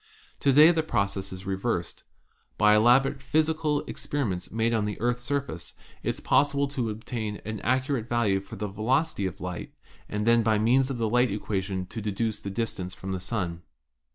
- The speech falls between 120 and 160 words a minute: No, average, 185 wpm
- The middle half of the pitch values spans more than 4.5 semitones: Yes, average, 4.9 semitones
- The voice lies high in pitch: No, low, 110 Hz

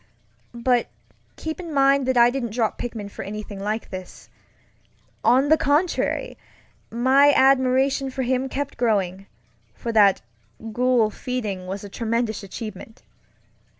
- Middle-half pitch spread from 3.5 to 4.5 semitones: Yes, average, 4.0 semitones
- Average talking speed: No, slow, 130 wpm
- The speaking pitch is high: Yes, high, 240 Hz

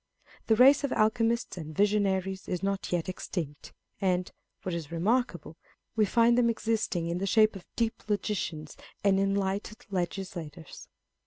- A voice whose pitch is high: Yes, high, 195 Hz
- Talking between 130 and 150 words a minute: Yes, average, 145 wpm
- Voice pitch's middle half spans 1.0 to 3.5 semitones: No, average, 3.9 semitones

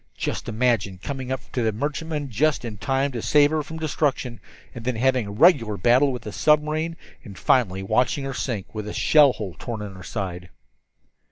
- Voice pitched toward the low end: Yes, low, 125 Hz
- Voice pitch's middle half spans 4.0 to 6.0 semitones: Yes, wide, 5.4 semitones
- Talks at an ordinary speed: Yes, average, 195 wpm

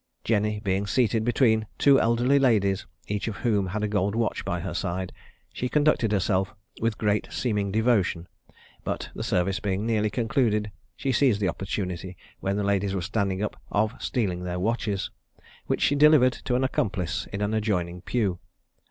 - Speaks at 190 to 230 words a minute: No, average, 170 wpm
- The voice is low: Yes, low, 105 Hz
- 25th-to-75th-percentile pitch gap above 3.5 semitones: No, average, 3.1 semitones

